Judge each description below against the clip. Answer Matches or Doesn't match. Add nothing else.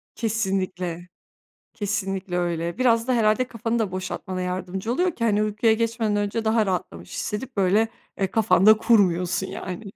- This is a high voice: Matches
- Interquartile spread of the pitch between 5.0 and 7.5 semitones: Doesn't match